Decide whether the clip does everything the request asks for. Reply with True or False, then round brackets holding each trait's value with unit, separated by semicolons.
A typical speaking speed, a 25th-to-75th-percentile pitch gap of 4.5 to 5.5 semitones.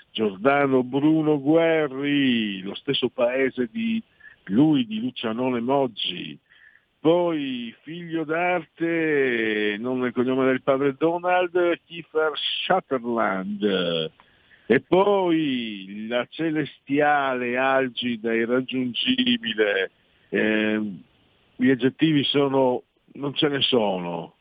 False (90 wpm; 5.1 semitones)